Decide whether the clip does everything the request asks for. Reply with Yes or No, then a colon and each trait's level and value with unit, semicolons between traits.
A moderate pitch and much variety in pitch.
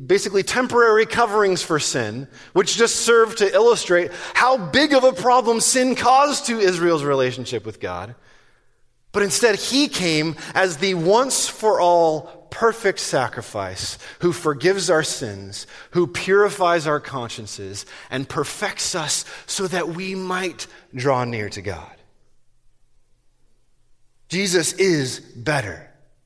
Yes: medium, 175 Hz; wide, 8.1 semitones